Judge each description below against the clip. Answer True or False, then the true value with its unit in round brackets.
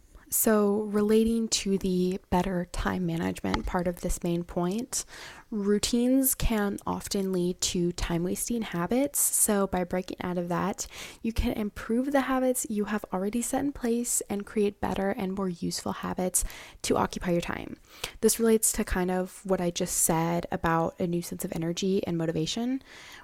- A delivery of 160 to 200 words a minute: True (170 wpm)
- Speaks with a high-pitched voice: True (195 Hz)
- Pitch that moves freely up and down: False (3.7 semitones)